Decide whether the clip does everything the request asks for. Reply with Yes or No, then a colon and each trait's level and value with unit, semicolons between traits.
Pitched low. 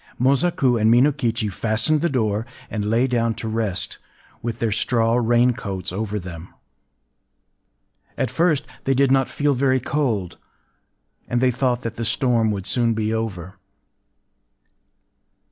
Yes: low, 115 Hz